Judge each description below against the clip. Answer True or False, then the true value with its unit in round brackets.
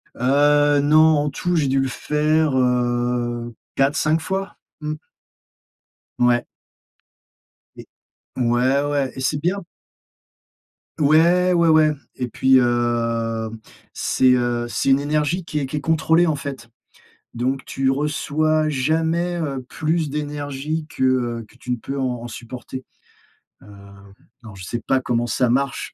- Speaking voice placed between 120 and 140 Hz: True (135 Hz)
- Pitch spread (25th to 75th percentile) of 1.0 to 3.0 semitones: False (4.0 semitones)